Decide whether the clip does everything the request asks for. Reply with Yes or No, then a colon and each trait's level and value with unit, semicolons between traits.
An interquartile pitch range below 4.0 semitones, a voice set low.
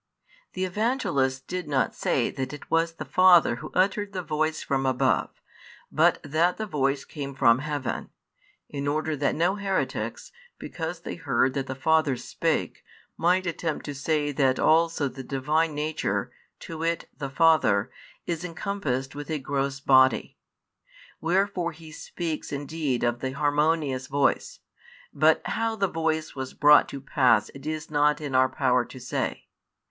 No: average, 3.5 semitones; medium, 150 Hz